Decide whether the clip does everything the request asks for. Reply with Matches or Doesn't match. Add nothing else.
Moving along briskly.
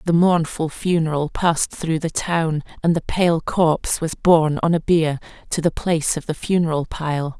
Doesn't match